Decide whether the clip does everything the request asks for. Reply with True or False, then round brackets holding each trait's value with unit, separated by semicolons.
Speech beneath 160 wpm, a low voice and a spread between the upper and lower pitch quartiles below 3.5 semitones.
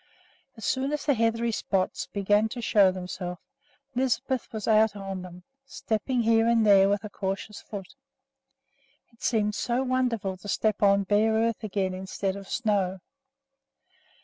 False (150 wpm; 210 Hz; 2.9 semitones)